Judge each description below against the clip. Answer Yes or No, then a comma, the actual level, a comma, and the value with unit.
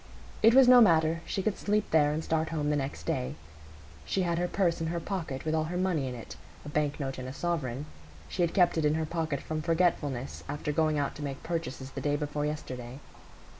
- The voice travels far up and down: No, average, 3.0 semitones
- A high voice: No, medium, 155 Hz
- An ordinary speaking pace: No, fast, 225 wpm